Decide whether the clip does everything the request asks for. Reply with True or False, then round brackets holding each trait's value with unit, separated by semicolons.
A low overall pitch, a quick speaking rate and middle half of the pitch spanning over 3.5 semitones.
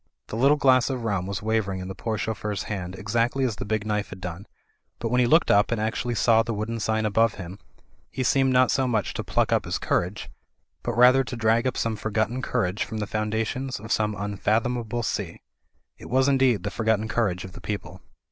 False (110 Hz; 215 wpm; 2.8 semitones)